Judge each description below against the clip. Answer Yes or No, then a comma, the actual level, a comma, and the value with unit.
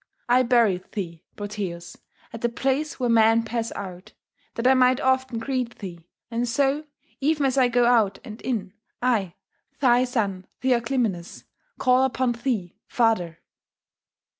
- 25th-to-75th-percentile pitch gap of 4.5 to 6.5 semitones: No, average, 4.0 semitones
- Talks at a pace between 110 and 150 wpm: Yes, average, 140 wpm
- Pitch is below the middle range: No, high, 235 Hz